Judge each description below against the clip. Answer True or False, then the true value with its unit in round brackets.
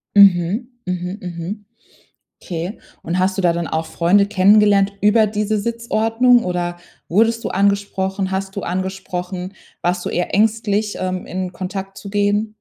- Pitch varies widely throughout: False (2.5 semitones)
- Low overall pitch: False (195 Hz)